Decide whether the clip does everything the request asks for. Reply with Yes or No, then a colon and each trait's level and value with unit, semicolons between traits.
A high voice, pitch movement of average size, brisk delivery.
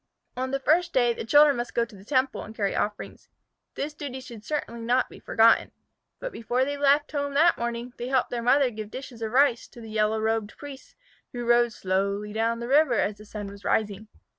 Yes: high, 240 Hz; average, 3.8 semitones; fast, 215 wpm